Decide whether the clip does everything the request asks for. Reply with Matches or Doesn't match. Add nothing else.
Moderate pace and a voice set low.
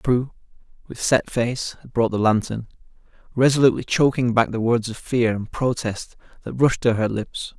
Matches